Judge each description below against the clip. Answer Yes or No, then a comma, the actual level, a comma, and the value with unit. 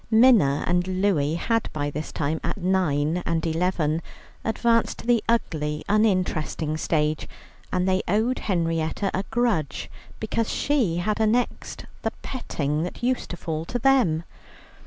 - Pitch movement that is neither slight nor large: No, wide, 6.0 semitones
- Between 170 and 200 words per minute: No, average, 140 wpm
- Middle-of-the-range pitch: Yes, medium, 180 Hz